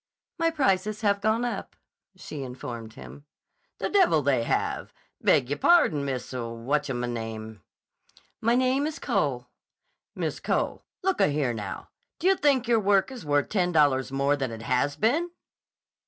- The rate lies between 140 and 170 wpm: Yes, average, 155 wpm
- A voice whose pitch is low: No, medium, 145 Hz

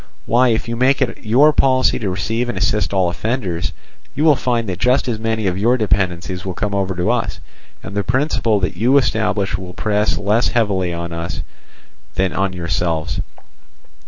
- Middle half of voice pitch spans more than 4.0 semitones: Yes, average, 4.5 semitones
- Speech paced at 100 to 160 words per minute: No, average, 185 wpm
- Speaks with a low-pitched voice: Yes, low, 105 Hz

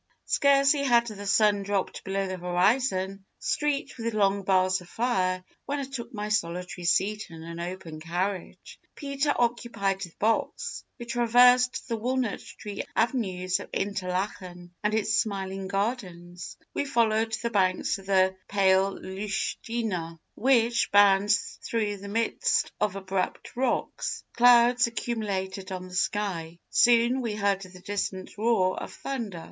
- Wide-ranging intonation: No, average, 3.9 semitones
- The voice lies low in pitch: No, high, 205 Hz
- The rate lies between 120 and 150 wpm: Yes, average, 140 wpm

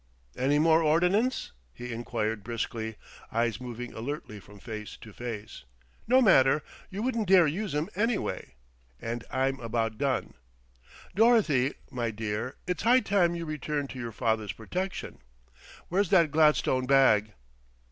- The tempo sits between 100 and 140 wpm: Yes, slow, 135 wpm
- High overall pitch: No, low, 135 Hz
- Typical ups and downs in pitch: No, wide, 7.2 semitones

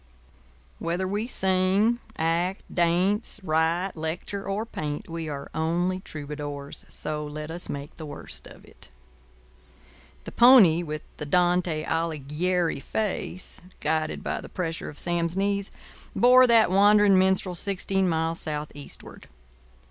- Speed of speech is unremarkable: No, slow, 125 wpm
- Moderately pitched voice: Yes, medium, 175 Hz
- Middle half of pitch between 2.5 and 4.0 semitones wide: Yes, average, 3.6 semitones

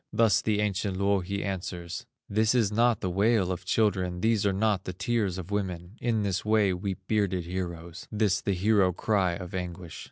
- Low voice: Yes, low, 100 Hz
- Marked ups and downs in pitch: No, average, 2.7 semitones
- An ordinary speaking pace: Yes, average, 185 wpm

